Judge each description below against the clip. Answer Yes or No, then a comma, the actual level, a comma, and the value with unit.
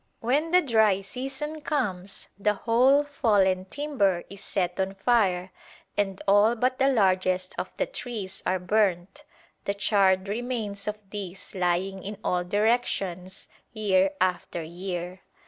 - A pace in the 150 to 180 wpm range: No, slow, 135 wpm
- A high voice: Yes, high, 200 Hz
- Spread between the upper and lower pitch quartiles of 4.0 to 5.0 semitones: Yes, average, 4.3 semitones